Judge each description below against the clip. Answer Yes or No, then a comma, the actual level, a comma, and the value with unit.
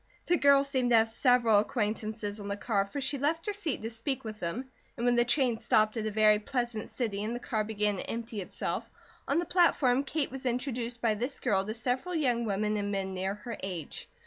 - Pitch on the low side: No, high, 230 Hz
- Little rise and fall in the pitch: No, average, 3.7 semitones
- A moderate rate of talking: No, fast, 225 wpm